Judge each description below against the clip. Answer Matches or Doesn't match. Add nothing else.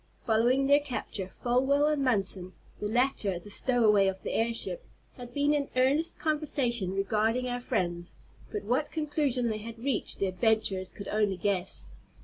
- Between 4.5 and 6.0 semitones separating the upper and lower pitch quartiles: Matches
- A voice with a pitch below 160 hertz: Doesn't match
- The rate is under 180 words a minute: Matches